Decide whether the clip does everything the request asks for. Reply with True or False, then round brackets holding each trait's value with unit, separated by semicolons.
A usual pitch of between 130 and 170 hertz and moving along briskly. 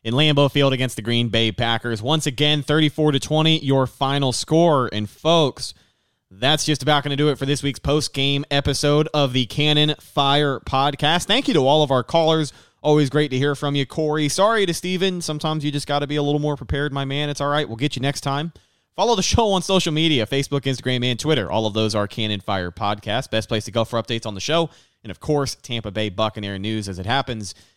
True (140 Hz; 230 wpm)